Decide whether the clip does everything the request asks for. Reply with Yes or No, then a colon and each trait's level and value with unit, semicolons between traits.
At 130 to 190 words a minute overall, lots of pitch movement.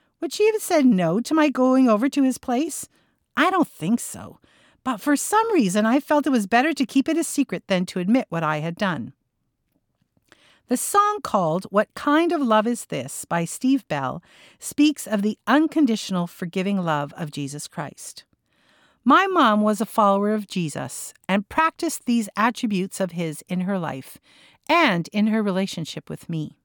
Yes: average, 180 wpm; wide, 7.2 semitones